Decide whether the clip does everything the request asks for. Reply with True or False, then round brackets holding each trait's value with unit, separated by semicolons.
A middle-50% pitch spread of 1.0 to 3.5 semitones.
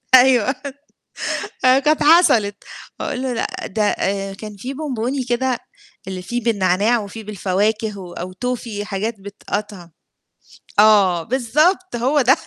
False (4.3 semitones)